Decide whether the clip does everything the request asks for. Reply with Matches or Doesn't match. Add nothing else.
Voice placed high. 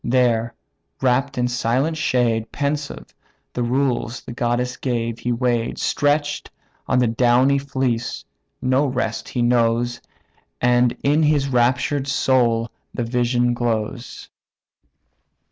Doesn't match